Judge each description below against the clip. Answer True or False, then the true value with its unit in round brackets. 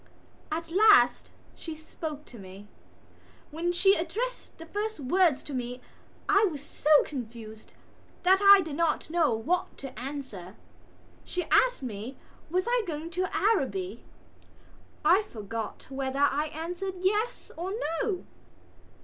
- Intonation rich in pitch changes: True (6.5 semitones)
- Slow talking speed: True (130 wpm)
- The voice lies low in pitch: False (315 Hz)